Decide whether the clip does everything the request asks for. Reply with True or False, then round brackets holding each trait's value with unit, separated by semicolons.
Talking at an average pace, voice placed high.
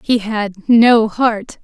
True (145 wpm; 225 Hz)